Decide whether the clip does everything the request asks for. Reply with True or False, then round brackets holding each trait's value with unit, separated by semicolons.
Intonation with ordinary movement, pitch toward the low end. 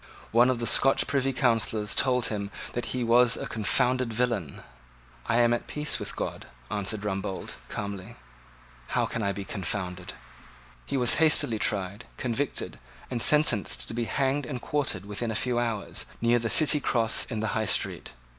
True (3.3 semitones; 115 Hz)